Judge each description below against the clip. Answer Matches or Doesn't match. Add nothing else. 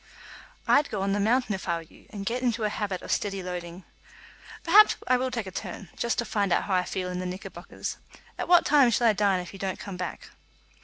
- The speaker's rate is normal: Doesn't match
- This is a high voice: Matches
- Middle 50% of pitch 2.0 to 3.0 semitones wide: Doesn't match